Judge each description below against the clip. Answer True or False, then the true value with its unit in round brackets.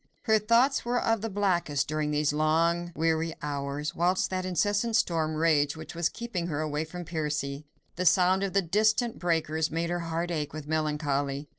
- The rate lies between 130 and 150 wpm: False (180 wpm)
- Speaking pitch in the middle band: True (165 Hz)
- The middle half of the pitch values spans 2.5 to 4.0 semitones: True (3.4 semitones)